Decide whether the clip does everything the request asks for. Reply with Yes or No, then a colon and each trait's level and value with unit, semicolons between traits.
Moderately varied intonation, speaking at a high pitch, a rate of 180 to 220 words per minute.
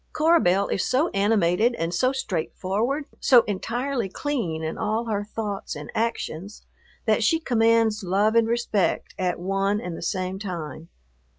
No: average, 4.2 semitones; high, 210 Hz; average, 155 wpm